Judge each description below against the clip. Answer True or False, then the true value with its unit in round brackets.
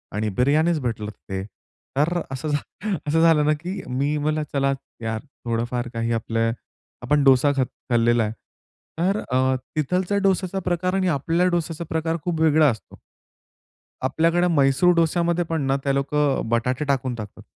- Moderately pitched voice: True (150 Hz)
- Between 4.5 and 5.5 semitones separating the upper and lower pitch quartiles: True (5.0 semitones)